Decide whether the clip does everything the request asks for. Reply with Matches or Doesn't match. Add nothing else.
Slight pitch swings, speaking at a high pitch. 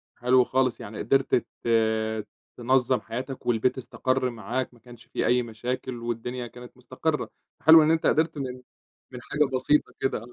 Doesn't match